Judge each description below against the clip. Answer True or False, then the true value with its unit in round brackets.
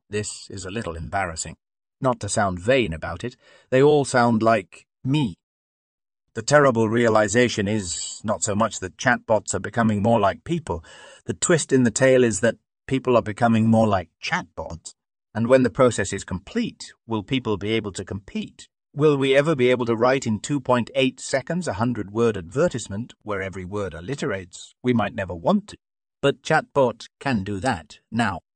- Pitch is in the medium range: False (115 Hz)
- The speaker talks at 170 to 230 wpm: True (175 wpm)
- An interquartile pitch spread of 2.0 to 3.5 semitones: False (4.5 semitones)